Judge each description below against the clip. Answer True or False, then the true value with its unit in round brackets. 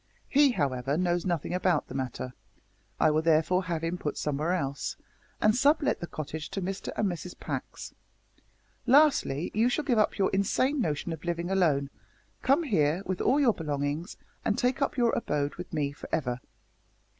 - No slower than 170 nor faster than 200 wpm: True (180 wpm)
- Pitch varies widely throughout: True (6.5 semitones)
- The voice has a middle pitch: True (175 Hz)